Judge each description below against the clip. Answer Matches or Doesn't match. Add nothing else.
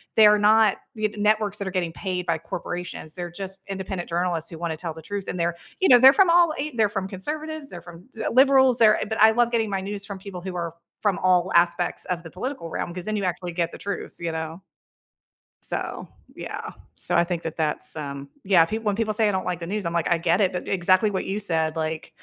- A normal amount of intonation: Matches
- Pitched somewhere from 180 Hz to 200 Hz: Matches